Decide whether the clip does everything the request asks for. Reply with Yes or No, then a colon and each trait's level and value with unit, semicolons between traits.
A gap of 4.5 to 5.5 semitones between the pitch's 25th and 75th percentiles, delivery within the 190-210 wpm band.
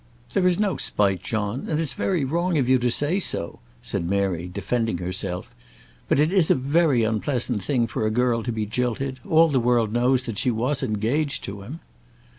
Yes: average, 5.2 semitones; average, 200 wpm